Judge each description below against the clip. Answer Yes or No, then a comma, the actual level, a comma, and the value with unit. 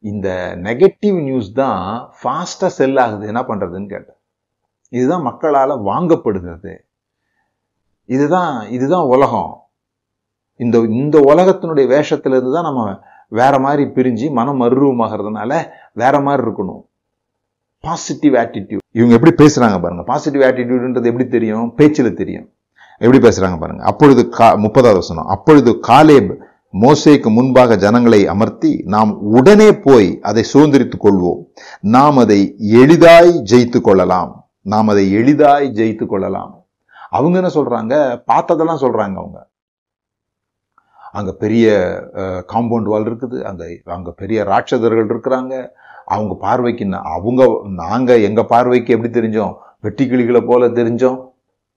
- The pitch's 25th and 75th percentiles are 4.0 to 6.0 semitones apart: Yes, average, 4.3 semitones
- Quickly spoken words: No, average, 115 wpm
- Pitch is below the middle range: Yes, low, 120 Hz